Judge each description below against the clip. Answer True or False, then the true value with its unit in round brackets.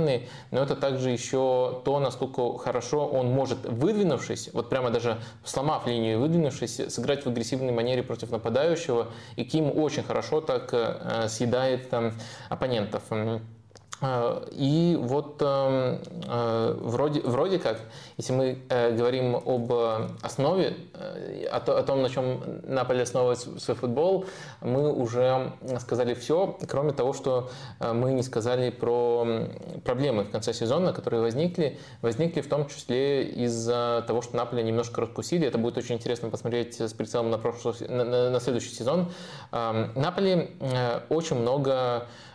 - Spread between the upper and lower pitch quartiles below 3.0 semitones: True (2.6 semitones)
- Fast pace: False (135 wpm)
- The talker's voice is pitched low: True (125 Hz)